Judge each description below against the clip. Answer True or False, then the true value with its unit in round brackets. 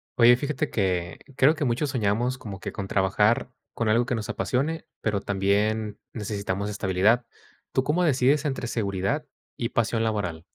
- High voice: False (110 Hz)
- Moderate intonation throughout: True (4.1 semitones)